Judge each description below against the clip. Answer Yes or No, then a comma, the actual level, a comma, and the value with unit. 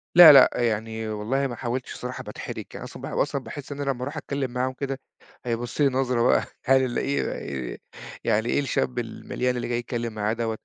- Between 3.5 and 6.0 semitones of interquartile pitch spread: No, narrow, 2.4 semitones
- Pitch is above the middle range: No, low, 125 Hz